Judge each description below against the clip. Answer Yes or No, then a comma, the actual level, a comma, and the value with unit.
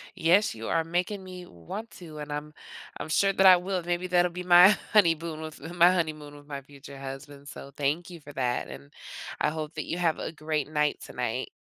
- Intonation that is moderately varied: Yes, average, 3.4 semitones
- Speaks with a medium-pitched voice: Yes, medium, 160 Hz